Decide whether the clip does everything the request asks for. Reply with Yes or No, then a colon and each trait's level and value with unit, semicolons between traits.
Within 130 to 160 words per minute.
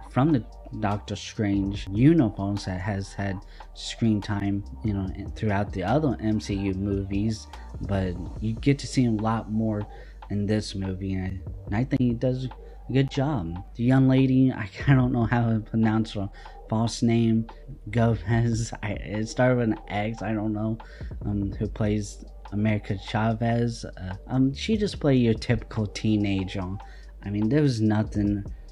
No: average, 175 wpm